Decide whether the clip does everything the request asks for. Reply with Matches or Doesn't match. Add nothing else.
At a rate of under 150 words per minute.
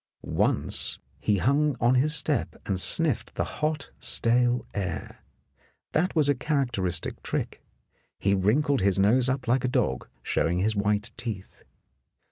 Matches